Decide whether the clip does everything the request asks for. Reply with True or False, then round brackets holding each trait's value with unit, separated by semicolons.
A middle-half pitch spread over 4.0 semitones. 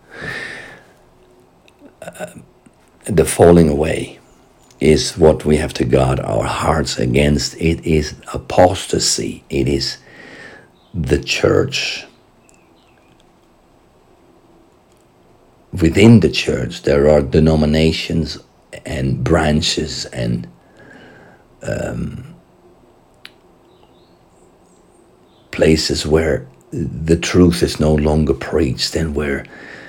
False (2.7 semitones)